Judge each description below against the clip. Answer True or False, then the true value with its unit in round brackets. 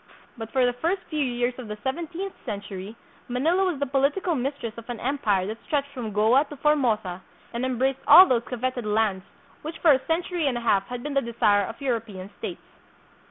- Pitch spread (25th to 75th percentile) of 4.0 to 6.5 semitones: True (4.5 semitones)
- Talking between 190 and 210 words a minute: True (200 wpm)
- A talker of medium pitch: False (250 Hz)